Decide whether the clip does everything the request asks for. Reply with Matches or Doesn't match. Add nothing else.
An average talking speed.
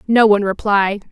Matches